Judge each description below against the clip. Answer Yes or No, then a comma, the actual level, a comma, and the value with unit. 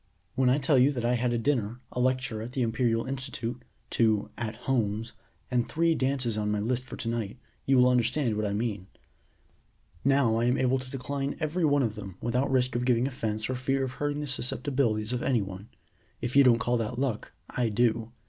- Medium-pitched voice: No, low, 125 Hz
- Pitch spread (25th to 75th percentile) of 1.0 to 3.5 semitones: Yes, average, 2.7 semitones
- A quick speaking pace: Yes, fast, 215 wpm